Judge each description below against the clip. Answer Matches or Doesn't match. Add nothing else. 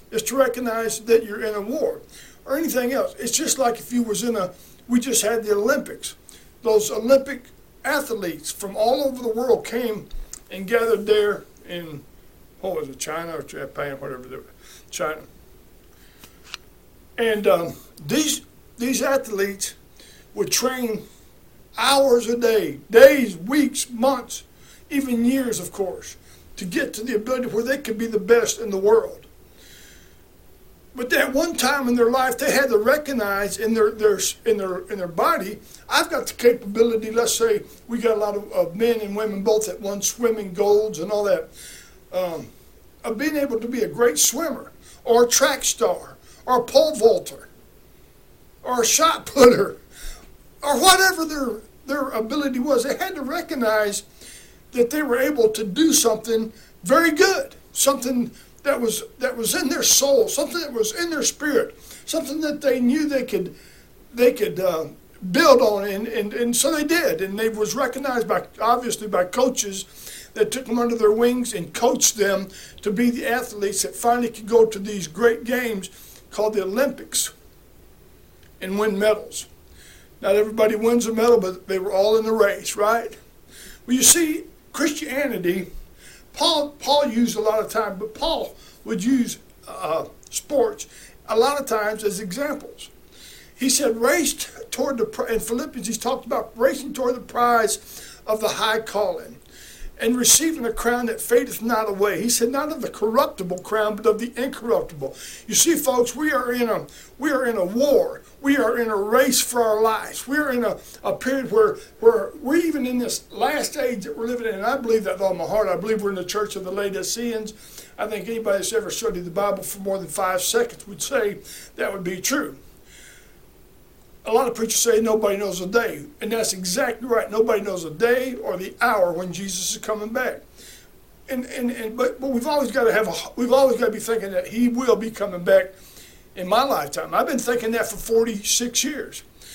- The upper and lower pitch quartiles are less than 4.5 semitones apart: Matches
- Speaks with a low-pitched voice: Doesn't match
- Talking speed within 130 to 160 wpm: Doesn't match